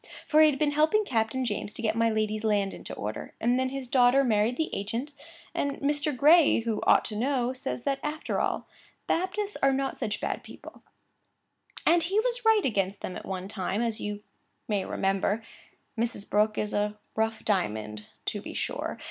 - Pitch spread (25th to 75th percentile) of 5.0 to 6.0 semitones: Yes, wide, 5.4 semitones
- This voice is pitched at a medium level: No, high, 235 Hz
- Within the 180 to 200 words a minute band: Yes, average, 190 wpm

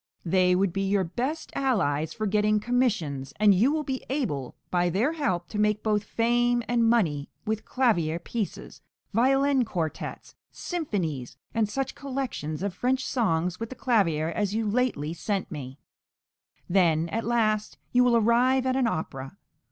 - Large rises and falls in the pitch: Yes, wide, 6.1 semitones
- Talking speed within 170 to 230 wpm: No, average, 160 wpm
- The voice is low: No, high, 210 Hz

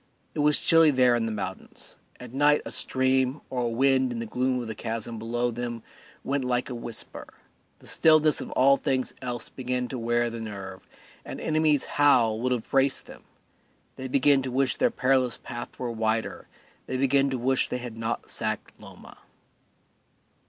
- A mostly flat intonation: Yes, narrow, 2.3 semitones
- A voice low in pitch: Yes, low, 125 Hz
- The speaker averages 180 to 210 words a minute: Yes, average, 185 wpm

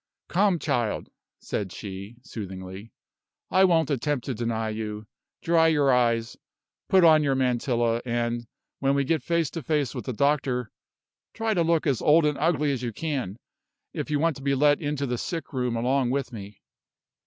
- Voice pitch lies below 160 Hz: Yes, low, 135 Hz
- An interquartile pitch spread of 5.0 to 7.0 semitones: No, average, 4.6 semitones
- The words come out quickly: No, average, 175 wpm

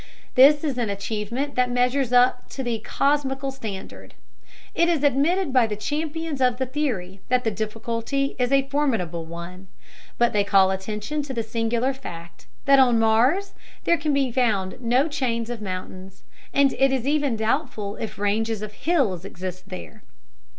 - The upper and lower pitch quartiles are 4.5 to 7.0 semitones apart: Yes, average, 4.8 semitones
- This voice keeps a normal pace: Yes, average, 165 wpm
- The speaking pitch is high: Yes, high, 245 Hz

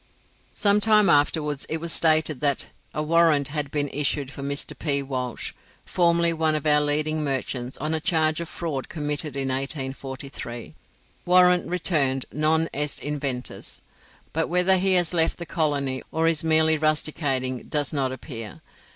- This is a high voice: No, medium, 150 Hz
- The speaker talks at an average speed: Yes, average, 155 wpm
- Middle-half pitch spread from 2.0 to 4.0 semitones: Yes, average, 2.9 semitones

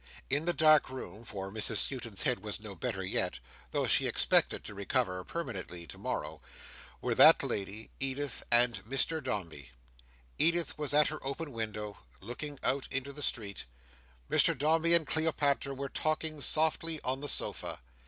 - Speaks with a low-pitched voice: Yes, low, 130 Hz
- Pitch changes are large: Yes, wide, 6.3 semitones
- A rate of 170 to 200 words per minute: No, average, 155 wpm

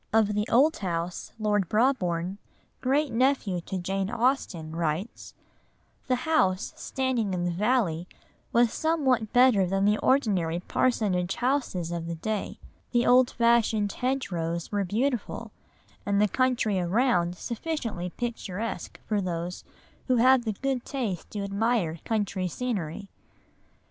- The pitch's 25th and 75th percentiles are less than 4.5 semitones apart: No, wide, 5.6 semitones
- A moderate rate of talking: No, slow, 130 wpm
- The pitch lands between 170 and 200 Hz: No, high, 210 Hz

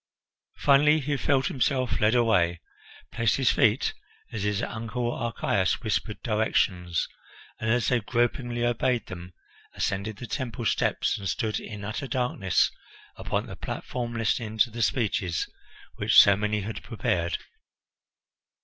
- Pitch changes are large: No, average, 3.0 semitones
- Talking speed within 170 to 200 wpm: No, slow, 135 wpm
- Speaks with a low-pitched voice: Yes, low, 115 Hz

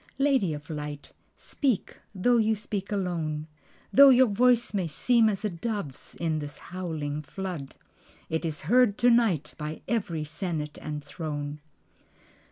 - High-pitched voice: No, medium, 175 Hz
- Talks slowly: No, average, 145 wpm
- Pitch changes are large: Yes, wide, 6.6 semitones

